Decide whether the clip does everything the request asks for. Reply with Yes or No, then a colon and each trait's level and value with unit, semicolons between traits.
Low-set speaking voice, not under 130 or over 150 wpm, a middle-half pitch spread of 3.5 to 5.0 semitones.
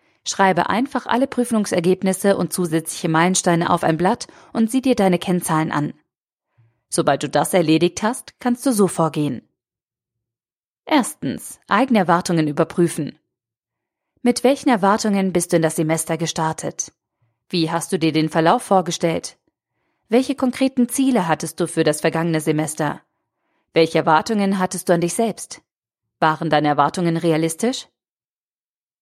No: medium, 170 Hz; average, 135 wpm; average, 4.6 semitones